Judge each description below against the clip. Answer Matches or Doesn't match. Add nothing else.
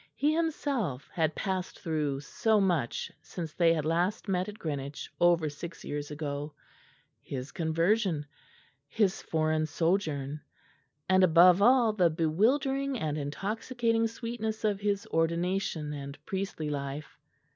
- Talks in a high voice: Doesn't match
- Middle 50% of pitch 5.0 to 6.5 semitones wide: Matches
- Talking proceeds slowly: Matches